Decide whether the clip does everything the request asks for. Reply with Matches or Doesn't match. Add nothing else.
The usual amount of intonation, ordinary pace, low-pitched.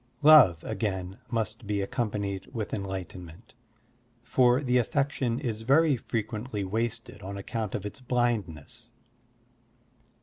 Doesn't match